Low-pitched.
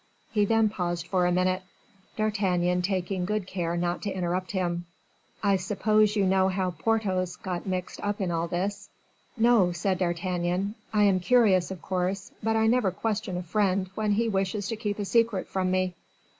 No: high, 190 Hz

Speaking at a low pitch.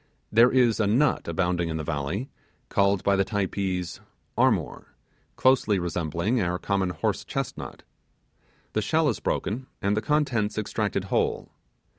Yes: low, 100 Hz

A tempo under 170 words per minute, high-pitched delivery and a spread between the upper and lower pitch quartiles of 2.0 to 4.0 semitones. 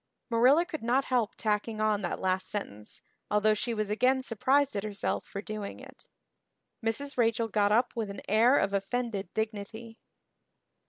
Yes: average, 160 wpm; high, 220 Hz; average, 2.9 semitones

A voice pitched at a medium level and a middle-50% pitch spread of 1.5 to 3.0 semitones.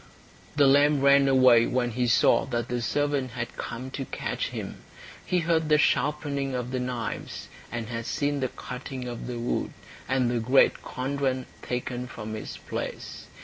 No: low, 130 Hz; narrow, 2.5 semitones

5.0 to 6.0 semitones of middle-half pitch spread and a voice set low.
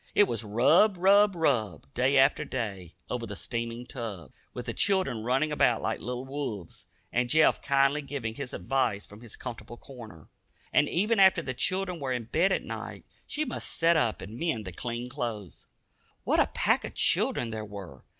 Yes: wide, 5.4 semitones; low, 125 Hz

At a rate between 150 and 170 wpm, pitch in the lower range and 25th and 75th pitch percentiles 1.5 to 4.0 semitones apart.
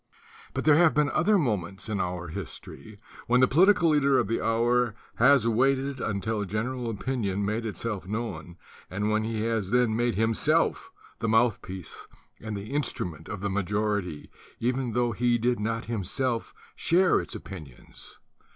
Yes: average, 160 wpm; low, 115 Hz; average, 3.5 semitones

